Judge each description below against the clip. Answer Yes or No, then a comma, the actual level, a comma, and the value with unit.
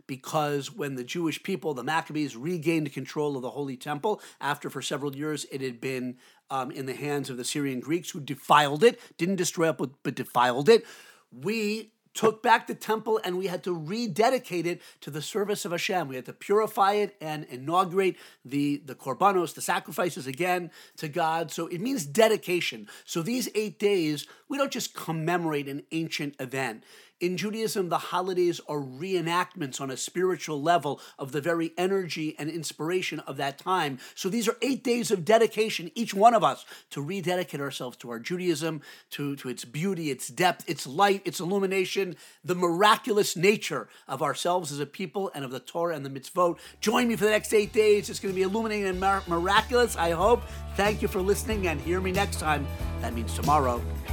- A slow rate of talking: No, average, 190 wpm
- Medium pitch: Yes, medium, 170 Hz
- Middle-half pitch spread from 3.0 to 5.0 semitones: No, wide, 5.5 semitones